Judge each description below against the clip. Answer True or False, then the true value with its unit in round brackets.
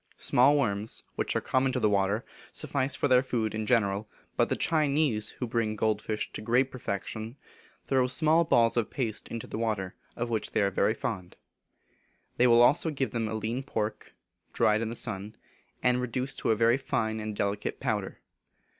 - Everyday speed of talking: True (180 wpm)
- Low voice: True (115 Hz)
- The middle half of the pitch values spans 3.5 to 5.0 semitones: False (3.1 semitones)